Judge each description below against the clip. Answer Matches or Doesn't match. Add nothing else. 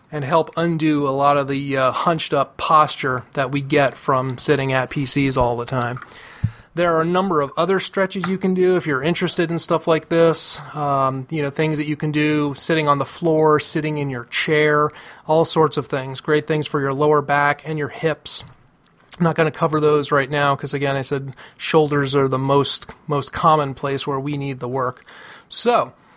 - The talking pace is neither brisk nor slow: Doesn't match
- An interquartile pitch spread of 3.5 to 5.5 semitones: Doesn't match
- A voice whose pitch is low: Doesn't match